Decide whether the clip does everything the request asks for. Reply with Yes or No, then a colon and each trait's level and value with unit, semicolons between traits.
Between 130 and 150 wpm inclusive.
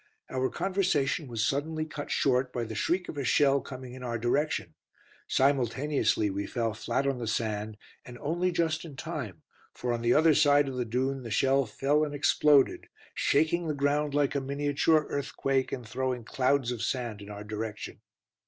No: average, 180 wpm